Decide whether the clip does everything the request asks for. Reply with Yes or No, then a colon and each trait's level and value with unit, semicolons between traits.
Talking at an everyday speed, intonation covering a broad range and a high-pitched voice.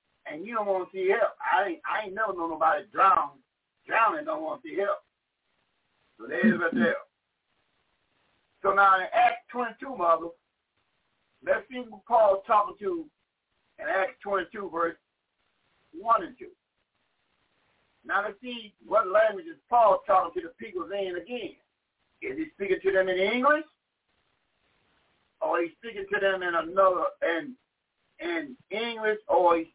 Yes: average, 155 wpm; wide, 8.8 semitones; high, 230 Hz